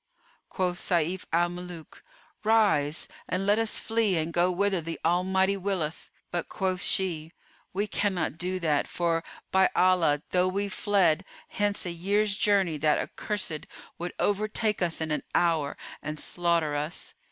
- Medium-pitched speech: Yes, medium, 180 Hz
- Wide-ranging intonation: No, average, 3.1 semitones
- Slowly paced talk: No, average, 150 wpm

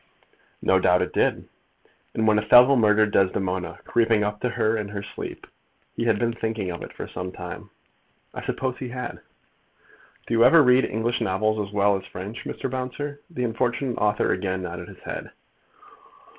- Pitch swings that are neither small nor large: Yes, average, 3.5 semitones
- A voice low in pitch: Yes, low, 110 Hz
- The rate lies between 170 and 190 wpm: Yes, average, 175 wpm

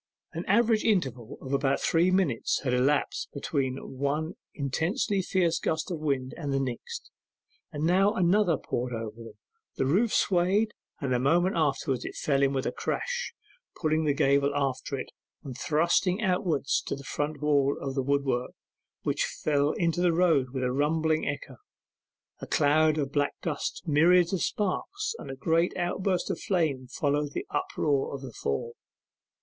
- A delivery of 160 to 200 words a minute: Yes, average, 165 wpm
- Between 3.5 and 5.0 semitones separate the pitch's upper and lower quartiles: Yes, average, 4.4 semitones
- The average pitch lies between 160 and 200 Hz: No, medium, 150 Hz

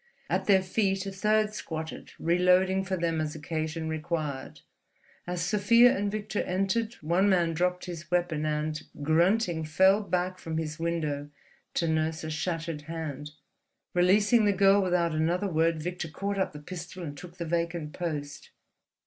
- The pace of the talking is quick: No, average, 155 wpm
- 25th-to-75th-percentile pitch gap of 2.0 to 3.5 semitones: Yes, average, 3.2 semitones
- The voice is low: No, medium, 170 Hz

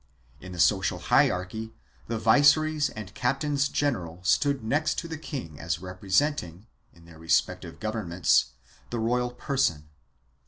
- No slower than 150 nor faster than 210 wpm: No, slow, 135 wpm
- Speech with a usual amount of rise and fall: No, wide, 7.9 semitones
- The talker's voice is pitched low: Yes, low, 110 Hz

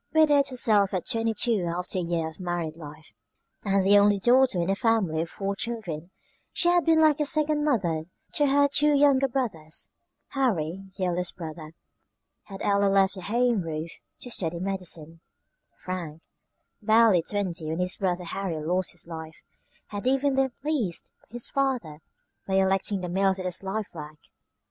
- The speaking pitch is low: No, high, 195 Hz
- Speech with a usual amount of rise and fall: No, wide, 6.0 semitones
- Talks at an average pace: Yes, average, 170 wpm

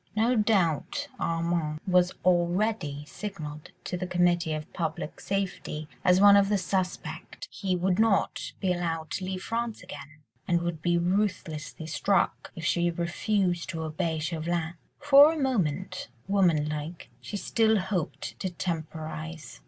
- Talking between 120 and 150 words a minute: Yes, slow, 135 wpm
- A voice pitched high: No, medium, 175 Hz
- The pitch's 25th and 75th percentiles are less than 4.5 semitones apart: Yes, average, 3.5 semitones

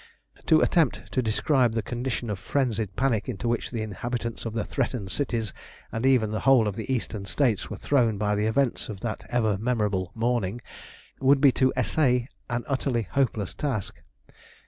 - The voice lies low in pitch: Yes, low, 115 Hz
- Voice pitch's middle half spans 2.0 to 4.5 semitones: Yes, average, 3.2 semitones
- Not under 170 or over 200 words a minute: Yes, average, 175 wpm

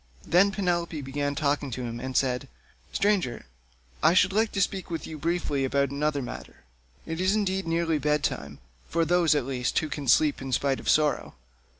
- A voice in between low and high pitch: Yes, medium, 150 Hz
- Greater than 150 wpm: Yes, average, 185 wpm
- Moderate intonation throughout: Yes, average, 4.5 semitones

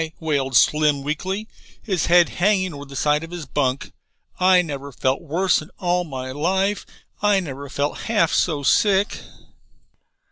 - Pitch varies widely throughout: No, average, 4.7 semitones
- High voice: No, medium, 160 Hz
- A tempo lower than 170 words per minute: Yes, average, 150 wpm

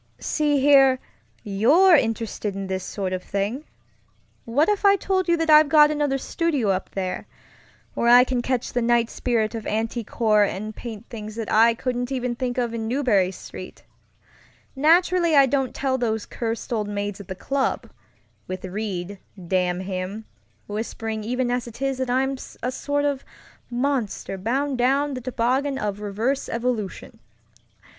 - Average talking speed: Yes, average, 160 wpm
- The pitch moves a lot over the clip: No, average, 4.4 semitones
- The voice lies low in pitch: No, high, 240 Hz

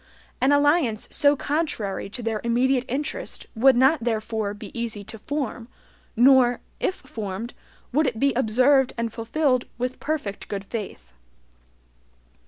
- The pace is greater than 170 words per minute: No, slow, 135 wpm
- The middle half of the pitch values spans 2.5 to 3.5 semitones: No, average, 3.9 semitones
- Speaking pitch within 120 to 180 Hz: No, high, 245 Hz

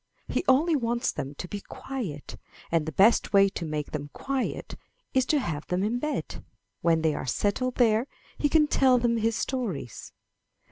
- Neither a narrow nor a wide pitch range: No, wide, 8.0 semitones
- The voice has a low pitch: No, high, 225 Hz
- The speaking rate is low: No, average, 180 wpm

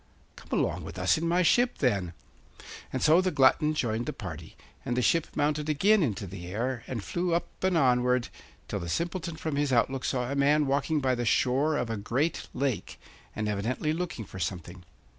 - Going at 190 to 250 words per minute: Yes, average, 200 wpm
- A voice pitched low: Yes, low, 130 Hz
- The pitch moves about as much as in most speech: No, wide, 5.8 semitones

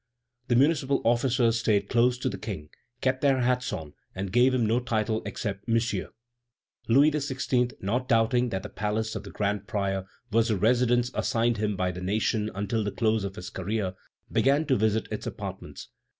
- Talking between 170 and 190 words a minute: Yes, average, 180 wpm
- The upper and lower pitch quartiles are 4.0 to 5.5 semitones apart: No, average, 3.4 semitones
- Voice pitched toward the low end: Yes, low, 115 Hz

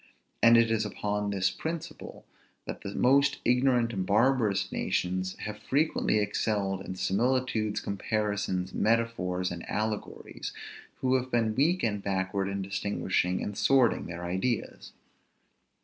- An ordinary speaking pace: No, slow, 130 wpm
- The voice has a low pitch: Yes, low, 105 Hz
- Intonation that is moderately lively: Yes, average, 3.8 semitones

